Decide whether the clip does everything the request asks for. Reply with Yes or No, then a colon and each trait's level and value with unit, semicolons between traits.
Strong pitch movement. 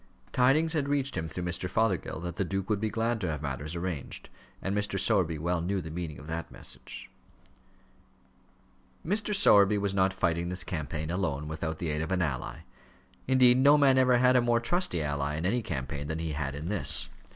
Yes: wide, 6.6 semitones